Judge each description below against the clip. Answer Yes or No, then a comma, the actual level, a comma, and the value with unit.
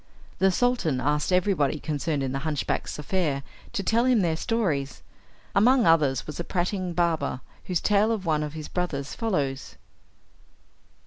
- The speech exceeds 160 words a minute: No, average, 150 wpm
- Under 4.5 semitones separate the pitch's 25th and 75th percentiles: No, average, 5.1 semitones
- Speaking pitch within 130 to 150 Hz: No, medium, 165 Hz